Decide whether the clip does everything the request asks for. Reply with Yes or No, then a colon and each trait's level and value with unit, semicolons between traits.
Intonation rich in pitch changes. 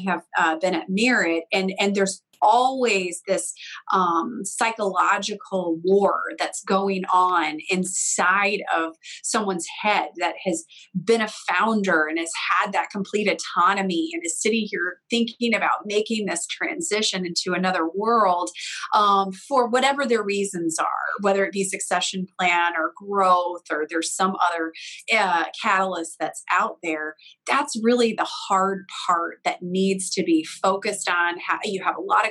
No: average, 3.0 semitones